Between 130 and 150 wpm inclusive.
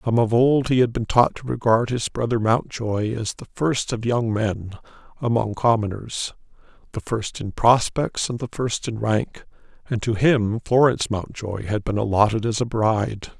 No: average, 175 wpm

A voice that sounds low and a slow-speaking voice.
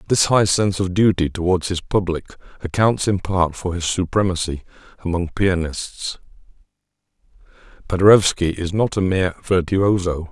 Yes: very low, 90 Hz; slow, 130 wpm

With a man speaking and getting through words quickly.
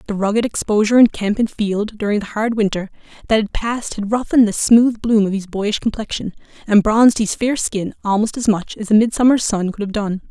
No: female; fast, 220 wpm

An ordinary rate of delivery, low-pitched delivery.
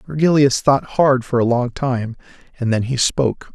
Yes: average, 185 wpm; low, 130 Hz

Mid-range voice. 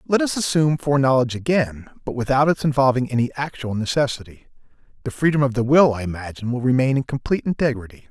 No: low, 130 Hz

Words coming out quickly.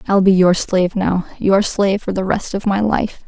Yes: fast, 240 wpm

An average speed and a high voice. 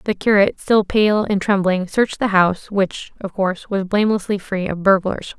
Yes: average, 190 wpm; high, 200 Hz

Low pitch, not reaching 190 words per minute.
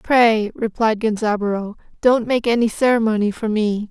No: high, 220 Hz; average, 140 wpm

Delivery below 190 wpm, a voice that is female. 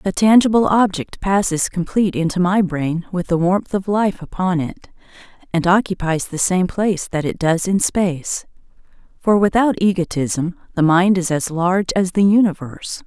Yes: average, 165 wpm; female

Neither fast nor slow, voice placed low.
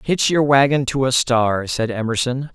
Yes: average, 190 wpm; low, 130 Hz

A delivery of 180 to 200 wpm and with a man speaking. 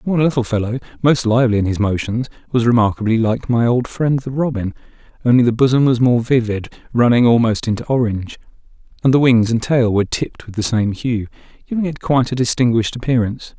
Yes: average, 190 wpm; male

